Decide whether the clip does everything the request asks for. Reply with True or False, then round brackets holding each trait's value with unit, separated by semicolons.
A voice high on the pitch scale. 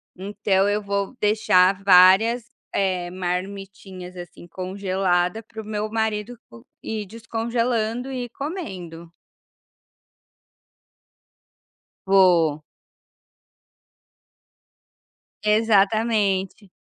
True (200 Hz)